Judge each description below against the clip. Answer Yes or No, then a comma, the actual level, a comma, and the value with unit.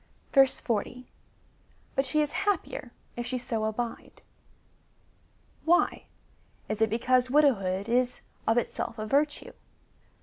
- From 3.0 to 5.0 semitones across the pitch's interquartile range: Yes, average, 3.5 semitones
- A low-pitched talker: No, high, 245 Hz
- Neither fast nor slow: No, slow, 115 wpm